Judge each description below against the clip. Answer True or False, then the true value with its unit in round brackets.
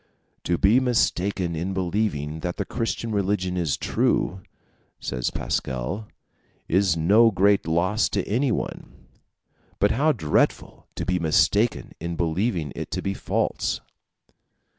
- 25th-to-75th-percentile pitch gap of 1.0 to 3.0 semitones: False (4.0 semitones)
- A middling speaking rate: False (125 wpm)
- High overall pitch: False (95 Hz)